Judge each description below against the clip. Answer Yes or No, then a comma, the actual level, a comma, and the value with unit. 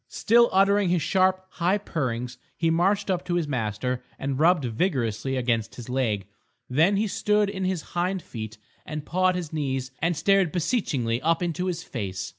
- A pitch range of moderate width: No, wide, 6.7 semitones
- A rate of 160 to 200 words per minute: Yes, average, 175 wpm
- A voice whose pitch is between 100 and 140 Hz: No, medium, 165 Hz